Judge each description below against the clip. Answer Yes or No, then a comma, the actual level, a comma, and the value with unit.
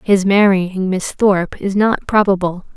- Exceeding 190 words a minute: No, average, 150 wpm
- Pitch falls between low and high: No, high, 195 Hz